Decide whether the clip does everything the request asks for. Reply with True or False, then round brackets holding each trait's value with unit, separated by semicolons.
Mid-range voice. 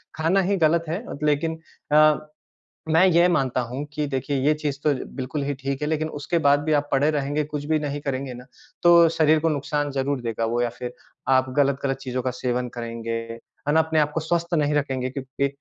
True (145 Hz)